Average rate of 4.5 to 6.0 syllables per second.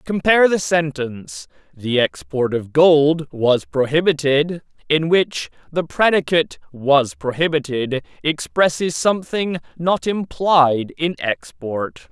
No: 3.9 syllables/s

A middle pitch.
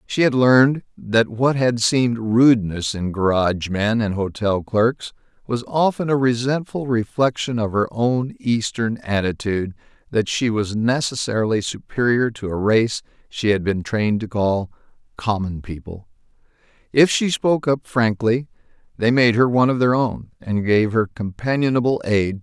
No: low, 115 Hz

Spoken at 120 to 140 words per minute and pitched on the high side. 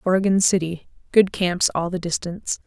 No: slow, 135 wpm; medium, 180 Hz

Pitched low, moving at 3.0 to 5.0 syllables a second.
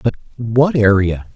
Yes: low, 110 Hz; 4.0 syllables/s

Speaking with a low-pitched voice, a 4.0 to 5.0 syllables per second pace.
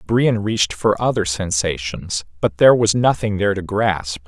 Yes: low, 100 Hz; 4.8 syllables/s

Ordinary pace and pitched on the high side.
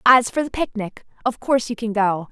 No: fast, 235 wpm; high, 230 Hz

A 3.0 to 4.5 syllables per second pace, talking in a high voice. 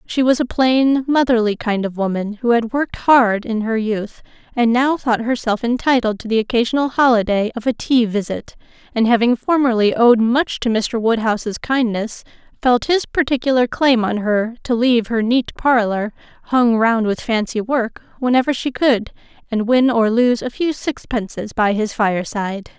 No: 4.8 syllables/s; high, 235 Hz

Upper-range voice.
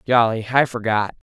No: low, 115 Hz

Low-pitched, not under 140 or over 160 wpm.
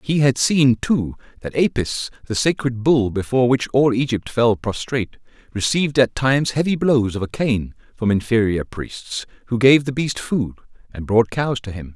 No: low, 120 Hz; average, 180 wpm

